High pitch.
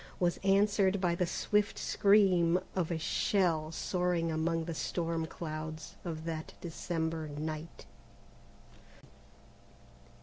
No: medium, 170 Hz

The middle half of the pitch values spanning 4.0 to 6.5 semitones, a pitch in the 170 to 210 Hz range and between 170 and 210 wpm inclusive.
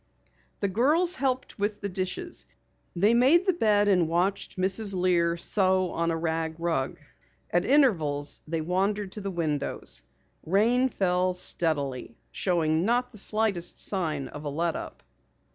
No: average, 4.4 semitones; medium, 185 Hz; average, 145 wpm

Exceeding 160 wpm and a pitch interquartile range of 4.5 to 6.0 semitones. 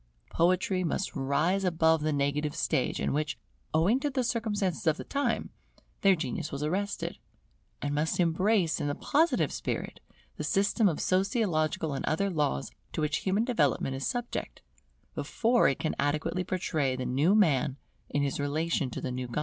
Yes: average, 170 wpm; average, 5.3 semitones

